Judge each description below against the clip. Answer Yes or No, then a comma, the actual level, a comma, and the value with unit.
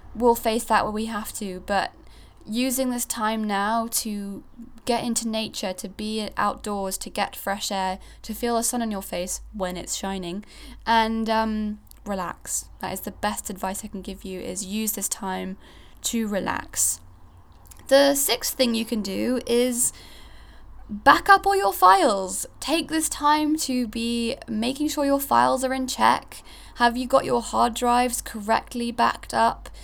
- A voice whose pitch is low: No, high, 220 Hz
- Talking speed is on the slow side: No, average, 170 wpm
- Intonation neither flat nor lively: Yes, average, 3.8 semitones